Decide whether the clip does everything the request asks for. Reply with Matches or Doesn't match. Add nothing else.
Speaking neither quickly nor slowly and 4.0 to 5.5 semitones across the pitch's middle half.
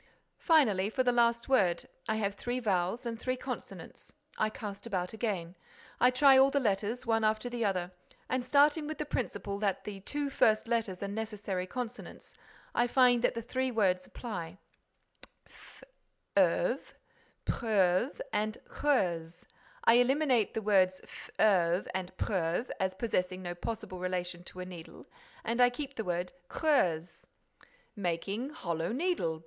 Matches